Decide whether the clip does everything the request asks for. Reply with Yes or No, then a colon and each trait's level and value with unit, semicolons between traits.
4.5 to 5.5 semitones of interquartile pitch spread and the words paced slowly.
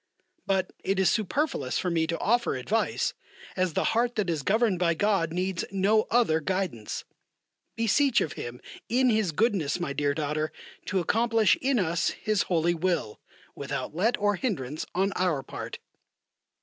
No: average, 5.2 semitones; average, 160 wpm